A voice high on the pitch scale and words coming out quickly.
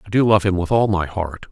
No: very low, 95 Hz; fast, 315 wpm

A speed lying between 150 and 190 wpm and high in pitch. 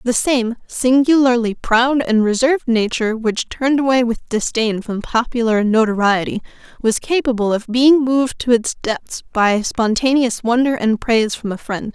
Yes: average, 155 wpm; high, 235 Hz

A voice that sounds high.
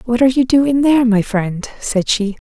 Yes: high, 235 Hz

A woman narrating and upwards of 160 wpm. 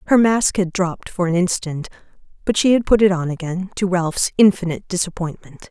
Yes: female; average, 190 wpm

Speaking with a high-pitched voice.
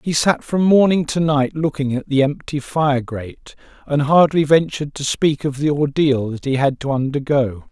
No: medium, 145 Hz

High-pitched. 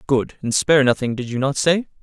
No: low, 135 Hz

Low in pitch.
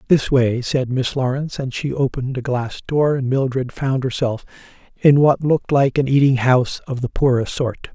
Yes: low, 130 Hz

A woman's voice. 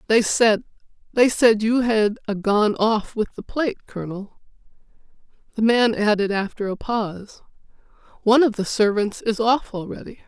Yes: female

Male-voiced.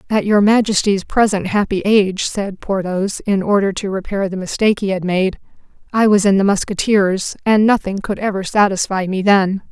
No: female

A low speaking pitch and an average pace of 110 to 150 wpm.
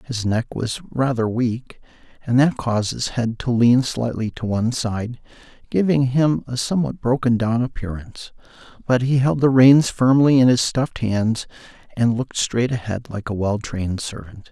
No: low, 120 Hz; average, 175 wpm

